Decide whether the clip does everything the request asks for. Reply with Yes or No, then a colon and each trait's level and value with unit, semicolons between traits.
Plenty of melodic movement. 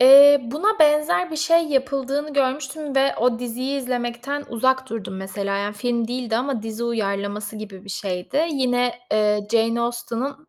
No: average, 4.0 semitones